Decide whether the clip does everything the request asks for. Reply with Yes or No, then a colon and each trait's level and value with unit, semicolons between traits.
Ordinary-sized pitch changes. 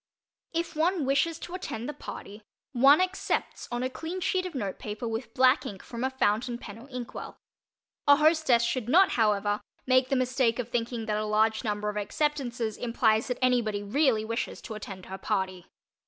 Yes: average, 4.2 semitones